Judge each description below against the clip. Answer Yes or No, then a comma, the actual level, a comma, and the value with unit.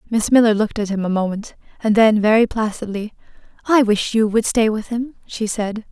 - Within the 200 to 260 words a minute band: Yes, fast, 205 wpm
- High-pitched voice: Yes, high, 215 Hz